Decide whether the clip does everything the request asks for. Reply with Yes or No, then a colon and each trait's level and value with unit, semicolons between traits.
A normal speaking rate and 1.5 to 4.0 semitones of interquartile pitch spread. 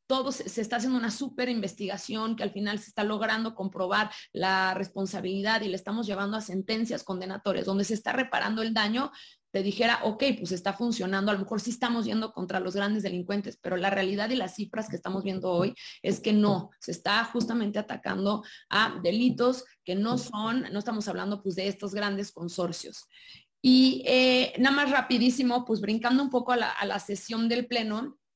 No: fast, 195 wpm; average, 3.6 semitones